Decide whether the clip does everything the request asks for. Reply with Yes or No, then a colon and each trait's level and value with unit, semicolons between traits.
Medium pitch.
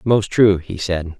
No: very low, 95 Hz